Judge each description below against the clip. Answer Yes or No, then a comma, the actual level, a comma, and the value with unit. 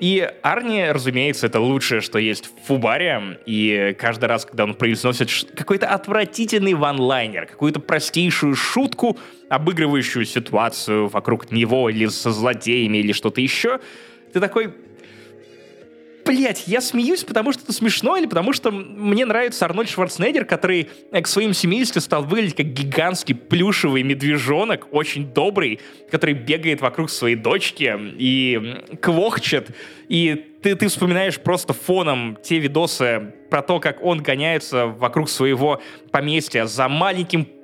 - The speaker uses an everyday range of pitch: No, wide, 7.1 semitones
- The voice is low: No, medium, 150 Hz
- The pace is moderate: Yes, average, 135 wpm